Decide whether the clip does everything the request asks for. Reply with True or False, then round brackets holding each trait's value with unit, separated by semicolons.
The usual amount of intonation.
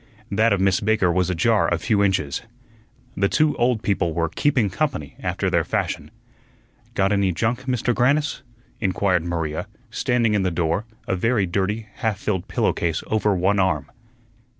True (4.1 semitones)